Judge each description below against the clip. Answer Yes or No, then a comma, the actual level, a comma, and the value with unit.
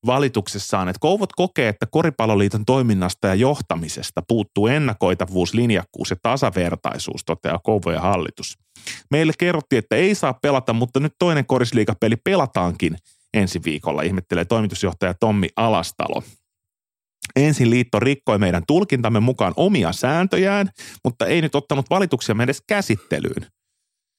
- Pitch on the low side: Yes, low, 110 Hz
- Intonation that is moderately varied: No, wide, 6.4 semitones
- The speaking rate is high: No, average, 120 wpm